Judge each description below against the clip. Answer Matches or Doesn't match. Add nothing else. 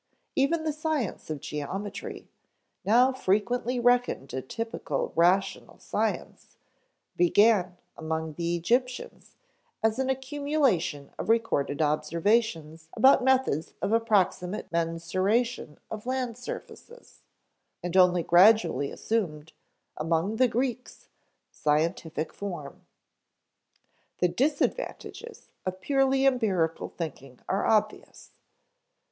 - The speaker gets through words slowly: Matches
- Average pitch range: Doesn't match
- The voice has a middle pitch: Doesn't match